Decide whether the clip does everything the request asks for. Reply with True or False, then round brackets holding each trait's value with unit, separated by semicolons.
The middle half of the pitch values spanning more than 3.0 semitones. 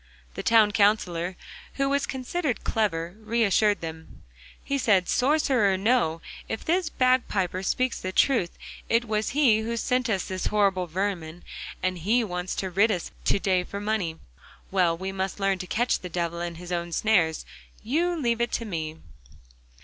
True (4.7 semitones)